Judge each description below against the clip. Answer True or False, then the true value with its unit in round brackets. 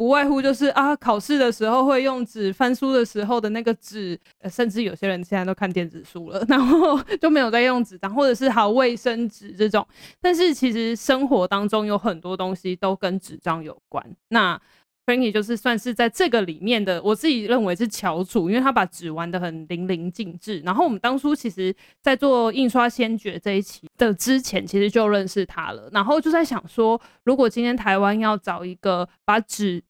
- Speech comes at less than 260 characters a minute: False (315 characters per minute)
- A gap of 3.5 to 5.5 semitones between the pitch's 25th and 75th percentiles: True (4.8 semitones)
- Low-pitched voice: False (225 Hz)